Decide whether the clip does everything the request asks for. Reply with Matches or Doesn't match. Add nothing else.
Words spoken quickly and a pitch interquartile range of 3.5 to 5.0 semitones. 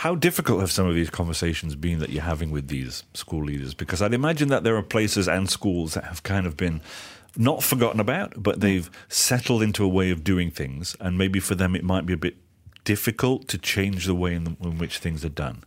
Matches